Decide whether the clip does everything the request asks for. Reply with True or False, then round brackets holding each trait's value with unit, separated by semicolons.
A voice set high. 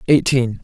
False (125 Hz)